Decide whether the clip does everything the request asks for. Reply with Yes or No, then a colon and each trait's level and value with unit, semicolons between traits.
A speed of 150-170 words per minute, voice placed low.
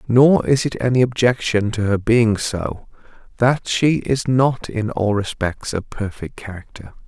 Yes: average, 160 wpm; low, 115 Hz